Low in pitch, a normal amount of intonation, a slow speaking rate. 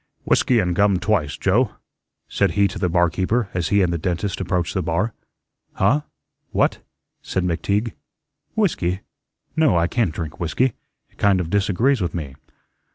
No: very low, 95 Hz; average, 3.5 semitones; average, 160 wpm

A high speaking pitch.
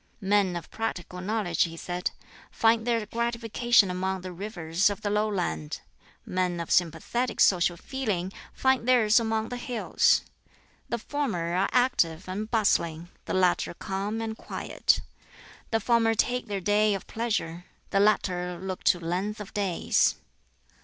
Yes: high, 205 Hz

